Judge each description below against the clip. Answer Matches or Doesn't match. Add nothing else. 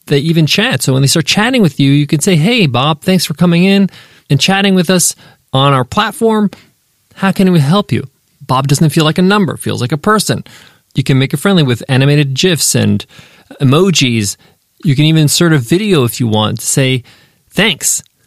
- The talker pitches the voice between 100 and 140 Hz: Doesn't match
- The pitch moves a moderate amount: Doesn't match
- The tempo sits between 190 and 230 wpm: Matches